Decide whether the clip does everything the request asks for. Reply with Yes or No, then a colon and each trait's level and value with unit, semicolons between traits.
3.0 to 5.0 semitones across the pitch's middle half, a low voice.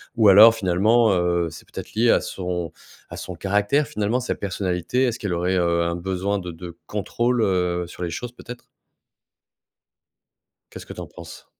Yes: average, 4.2 semitones; very low, 95 Hz